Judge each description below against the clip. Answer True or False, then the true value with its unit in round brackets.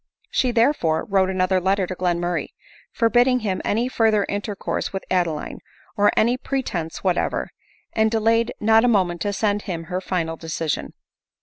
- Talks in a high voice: True (195 Hz)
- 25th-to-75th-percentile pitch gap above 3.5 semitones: True (4.1 semitones)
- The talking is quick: False (165 wpm)